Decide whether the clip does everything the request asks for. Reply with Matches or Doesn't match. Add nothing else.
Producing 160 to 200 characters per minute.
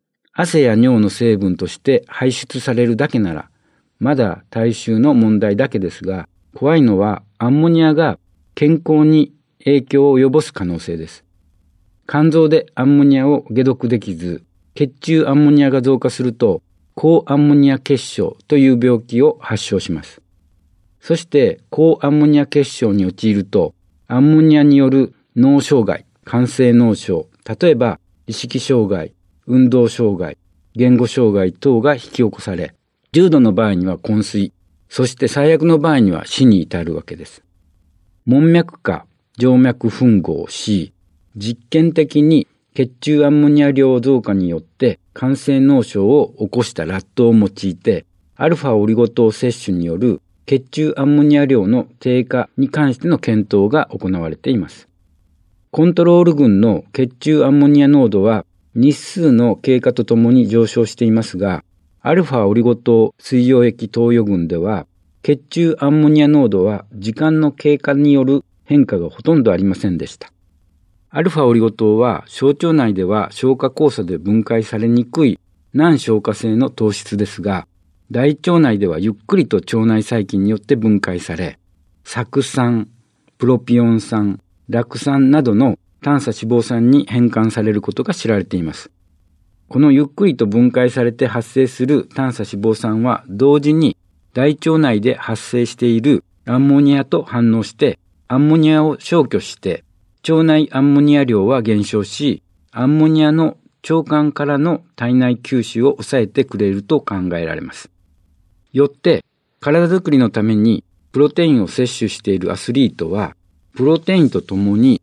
Doesn't match